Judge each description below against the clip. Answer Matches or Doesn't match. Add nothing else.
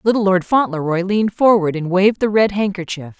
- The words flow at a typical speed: Matches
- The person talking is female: Matches